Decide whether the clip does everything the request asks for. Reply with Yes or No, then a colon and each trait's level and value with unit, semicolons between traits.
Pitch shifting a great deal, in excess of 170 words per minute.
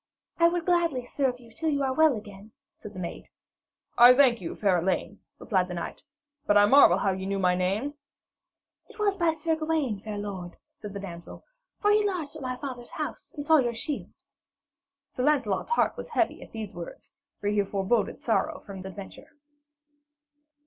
Yes: wide, 7.4 semitones; average, 190 wpm